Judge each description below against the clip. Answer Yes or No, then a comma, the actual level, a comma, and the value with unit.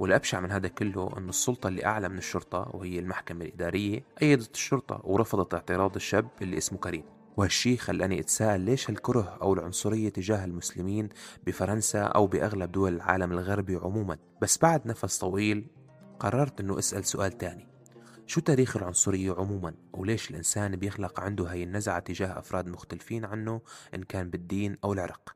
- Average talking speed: No, fast, 155 wpm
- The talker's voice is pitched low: Yes, low, 100 Hz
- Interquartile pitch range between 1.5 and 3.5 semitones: Yes, average, 2.8 semitones